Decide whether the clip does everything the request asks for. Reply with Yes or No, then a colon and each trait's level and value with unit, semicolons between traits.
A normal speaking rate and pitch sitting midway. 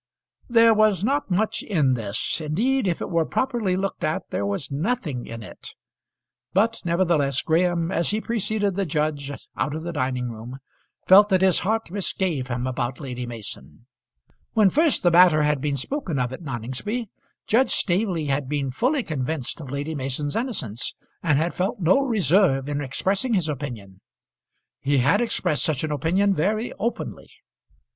Yes: average, 165 wpm; medium, 165 Hz